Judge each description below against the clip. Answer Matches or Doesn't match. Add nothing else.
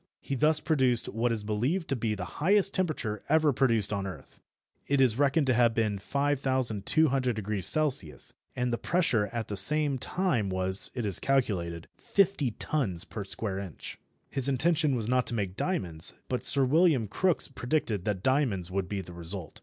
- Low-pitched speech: Matches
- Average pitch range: Doesn't match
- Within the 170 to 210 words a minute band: Matches